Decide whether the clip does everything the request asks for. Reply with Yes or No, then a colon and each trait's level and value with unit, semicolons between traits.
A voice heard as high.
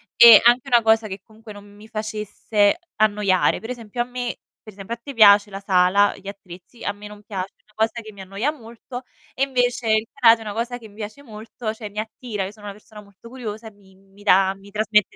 Yes: high, 215 Hz